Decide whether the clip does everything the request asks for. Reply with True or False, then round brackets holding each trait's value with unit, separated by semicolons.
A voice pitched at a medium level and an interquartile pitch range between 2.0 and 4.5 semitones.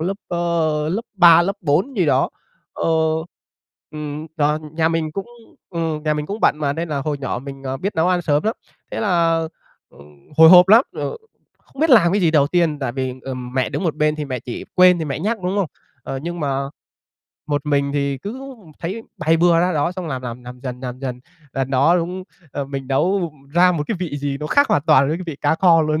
True (155 Hz; 4.0 semitones)